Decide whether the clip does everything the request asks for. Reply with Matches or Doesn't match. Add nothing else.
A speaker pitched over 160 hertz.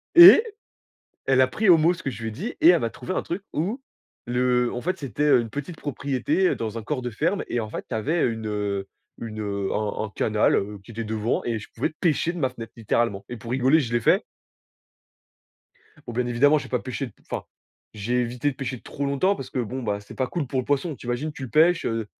Doesn't match